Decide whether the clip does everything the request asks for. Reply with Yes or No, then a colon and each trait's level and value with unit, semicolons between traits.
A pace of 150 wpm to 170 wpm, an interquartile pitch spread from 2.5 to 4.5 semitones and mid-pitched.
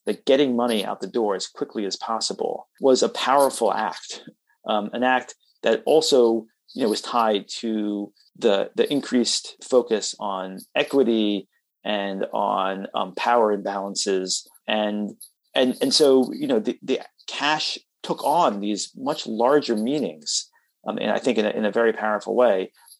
No: average, 160 wpm; average, 3.0 semitones; low, 105 Hz